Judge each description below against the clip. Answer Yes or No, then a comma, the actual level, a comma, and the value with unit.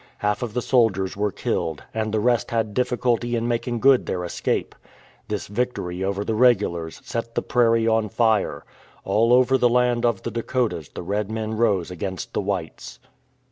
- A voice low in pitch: Yes, low, 115 Hz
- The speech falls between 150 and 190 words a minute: Yes, average, 180 wpm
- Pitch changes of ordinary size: Yes, average, 3.1 semitones